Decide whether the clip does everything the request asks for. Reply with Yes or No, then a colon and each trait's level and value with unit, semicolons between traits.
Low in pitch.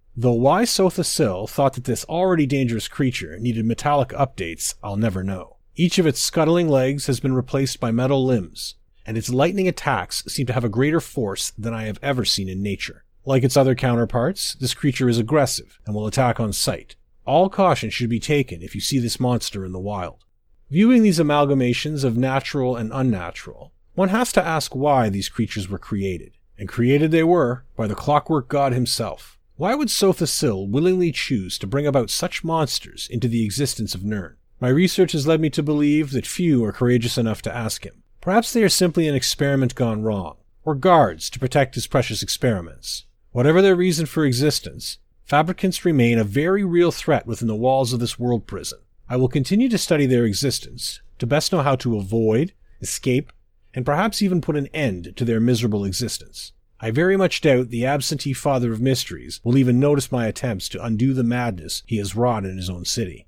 Yes: low, 125 Hz